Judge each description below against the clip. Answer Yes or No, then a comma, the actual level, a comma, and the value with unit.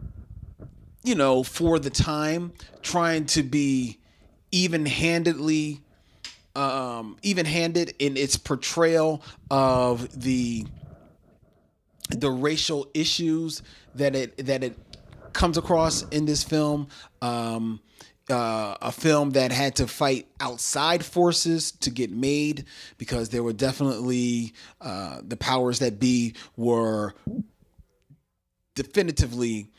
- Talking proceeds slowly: Yes, slow, 105 wpm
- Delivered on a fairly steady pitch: No, average, 4.4 semitones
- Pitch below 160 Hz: Yes, low, 135 Hz